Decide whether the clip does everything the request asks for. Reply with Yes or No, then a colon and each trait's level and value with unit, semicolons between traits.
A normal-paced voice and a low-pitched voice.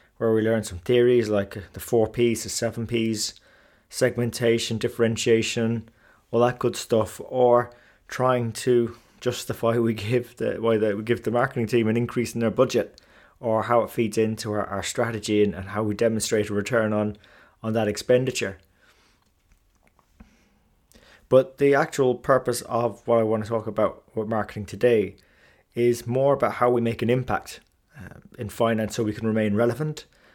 Yes: average, 170 wpm; low, 115 Hz